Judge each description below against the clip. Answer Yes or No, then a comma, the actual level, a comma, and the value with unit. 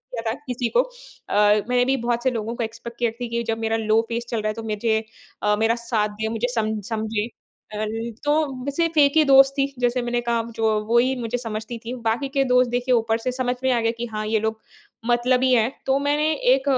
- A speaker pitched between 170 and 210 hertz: No, high, 235 Hz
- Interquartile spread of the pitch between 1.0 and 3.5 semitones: Yes, narrow, 2.4 semitones